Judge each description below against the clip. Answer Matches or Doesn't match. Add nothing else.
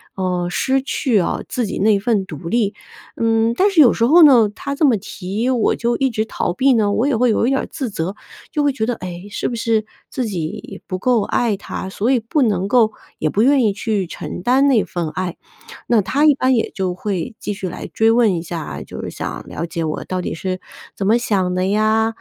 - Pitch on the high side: Matches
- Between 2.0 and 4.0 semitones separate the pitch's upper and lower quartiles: Doesn't match